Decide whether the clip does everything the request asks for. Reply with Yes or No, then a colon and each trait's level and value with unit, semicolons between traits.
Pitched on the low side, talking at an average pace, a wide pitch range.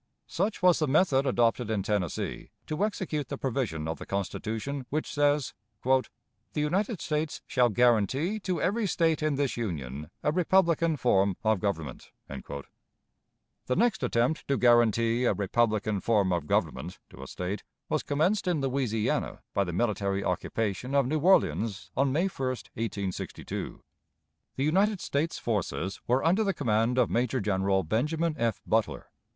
Yes: low, 125 Hz; average, 150 wpm; wide, 6.7 semitones